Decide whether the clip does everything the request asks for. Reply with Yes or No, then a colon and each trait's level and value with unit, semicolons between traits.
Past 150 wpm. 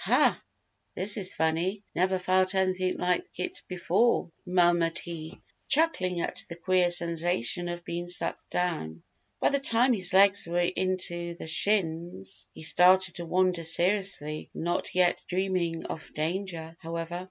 No: average, 145 wpm